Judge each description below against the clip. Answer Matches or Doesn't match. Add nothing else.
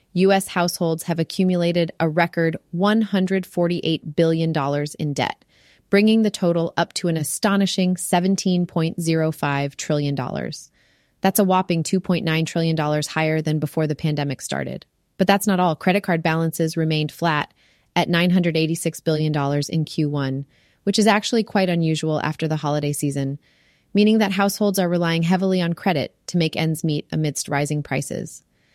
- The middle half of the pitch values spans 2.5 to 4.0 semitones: Matches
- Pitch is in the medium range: Matches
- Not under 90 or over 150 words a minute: Matches